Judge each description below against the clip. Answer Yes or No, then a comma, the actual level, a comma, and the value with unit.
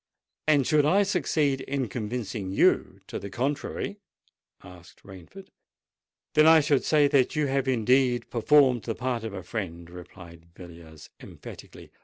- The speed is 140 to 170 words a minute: Yes, average, 145 wpm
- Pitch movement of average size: No, wide, 7.4 semitones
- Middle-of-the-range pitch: No, low, 125 Hz